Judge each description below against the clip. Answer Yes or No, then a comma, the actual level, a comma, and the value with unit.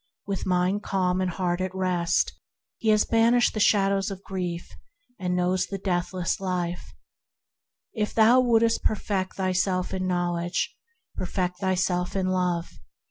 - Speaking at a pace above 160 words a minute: No, slow, 135 wpm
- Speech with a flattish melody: Yes, narrow, 1.8 semitones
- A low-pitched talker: No, medium, 185 Hz